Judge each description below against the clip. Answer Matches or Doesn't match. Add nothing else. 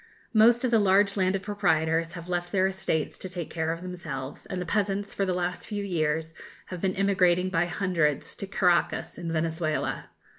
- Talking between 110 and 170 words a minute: Doesn't match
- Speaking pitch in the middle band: Matches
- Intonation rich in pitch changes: Doesn't match